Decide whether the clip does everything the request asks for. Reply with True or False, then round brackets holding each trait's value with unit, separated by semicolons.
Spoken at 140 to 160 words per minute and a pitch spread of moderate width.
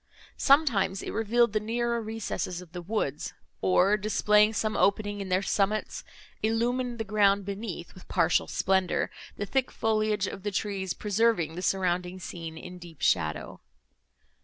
True (150 wpm; 3.3 semitones)